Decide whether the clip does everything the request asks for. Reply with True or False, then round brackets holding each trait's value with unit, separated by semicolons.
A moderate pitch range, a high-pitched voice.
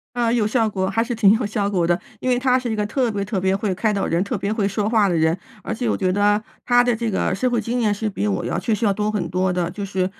True (3.1 semitones; 210 Hz)